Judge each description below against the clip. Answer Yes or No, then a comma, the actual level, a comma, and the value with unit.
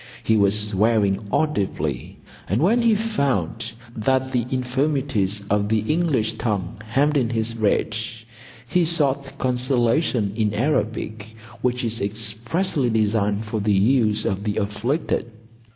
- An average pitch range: Yes, average, 4.1 semitones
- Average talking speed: No, slow, 130 wpm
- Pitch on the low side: Yes, low, 115 Hz